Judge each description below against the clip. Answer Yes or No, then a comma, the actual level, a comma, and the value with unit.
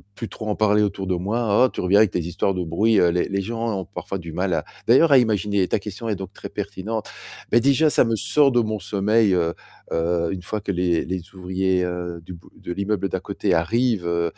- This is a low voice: Yes, low, 100 Hz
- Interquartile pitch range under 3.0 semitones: No, average, 3.4 semitones